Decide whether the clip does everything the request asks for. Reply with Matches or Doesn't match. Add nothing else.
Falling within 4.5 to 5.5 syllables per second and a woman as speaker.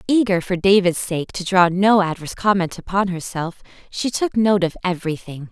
Matches